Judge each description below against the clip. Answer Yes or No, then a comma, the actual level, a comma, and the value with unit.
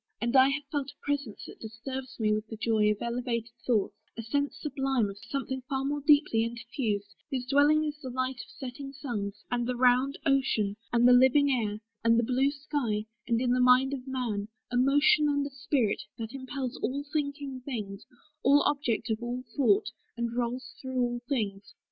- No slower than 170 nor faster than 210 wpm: Yes, average, 190 wpm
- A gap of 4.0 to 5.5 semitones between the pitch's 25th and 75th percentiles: No, average, 3.2 semitones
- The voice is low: No, very high, 250 Hz